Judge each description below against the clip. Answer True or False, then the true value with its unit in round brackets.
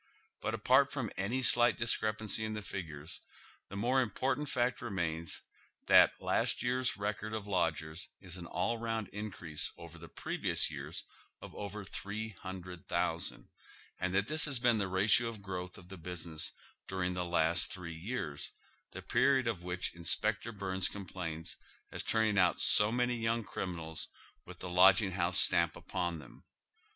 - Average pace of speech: True (160 wpm)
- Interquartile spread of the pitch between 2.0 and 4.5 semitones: True (4.2 semitones)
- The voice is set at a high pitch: False (95 Hz)